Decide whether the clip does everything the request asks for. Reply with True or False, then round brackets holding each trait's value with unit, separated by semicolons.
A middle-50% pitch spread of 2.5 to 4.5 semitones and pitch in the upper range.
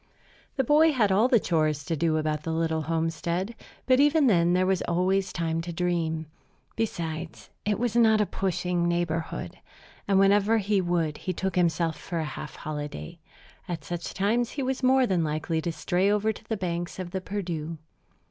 False (4.1 semitones; 175 Hz)